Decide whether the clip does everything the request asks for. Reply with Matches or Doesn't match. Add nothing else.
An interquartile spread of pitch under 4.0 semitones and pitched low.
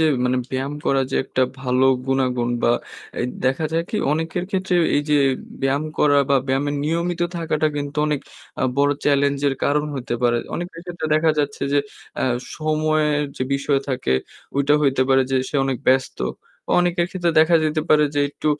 Doesn't match